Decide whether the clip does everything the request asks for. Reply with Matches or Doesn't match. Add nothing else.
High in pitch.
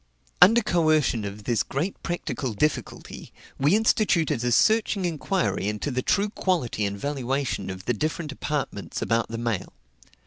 Doesn't match